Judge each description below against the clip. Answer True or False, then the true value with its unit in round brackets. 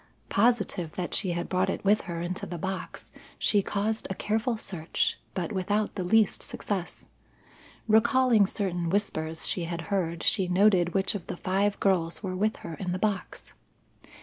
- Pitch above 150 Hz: True (190 Hz)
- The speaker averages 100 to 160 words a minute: False (170 wpm)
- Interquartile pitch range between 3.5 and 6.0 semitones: False (2.9 semitones)